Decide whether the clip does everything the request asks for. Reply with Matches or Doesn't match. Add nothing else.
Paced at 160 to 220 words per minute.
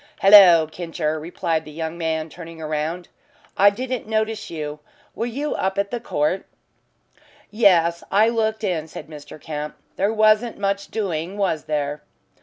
Doesn't match